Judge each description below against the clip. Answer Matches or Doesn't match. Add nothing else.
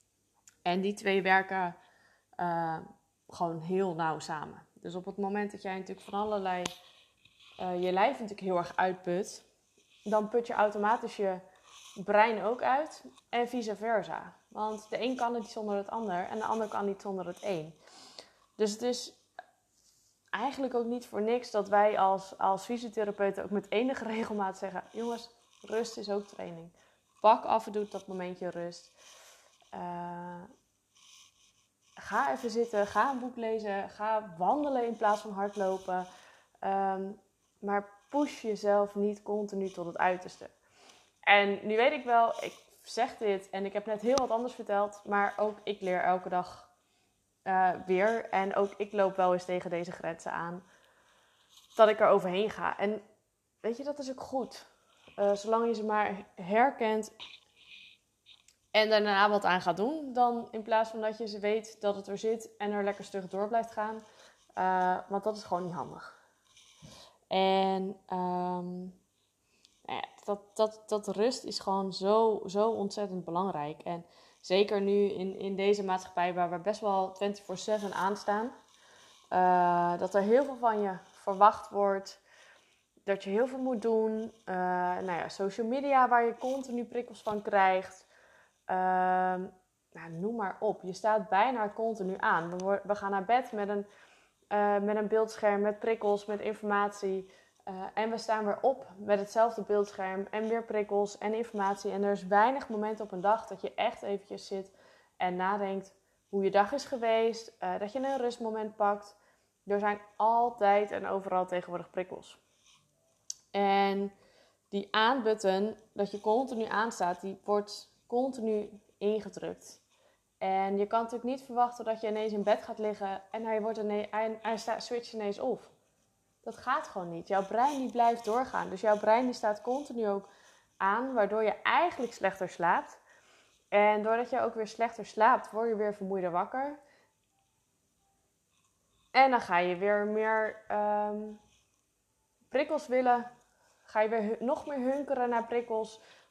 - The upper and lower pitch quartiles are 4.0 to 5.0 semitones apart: Doesn't match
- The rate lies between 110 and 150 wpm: Doesn't match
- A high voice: Matches